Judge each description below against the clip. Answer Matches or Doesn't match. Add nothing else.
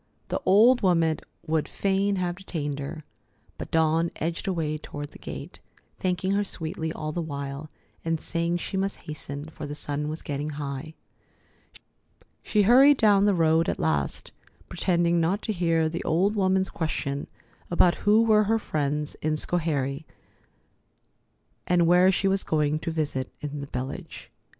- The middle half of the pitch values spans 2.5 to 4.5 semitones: Matches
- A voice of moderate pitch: Matches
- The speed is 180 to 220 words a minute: Doesn't match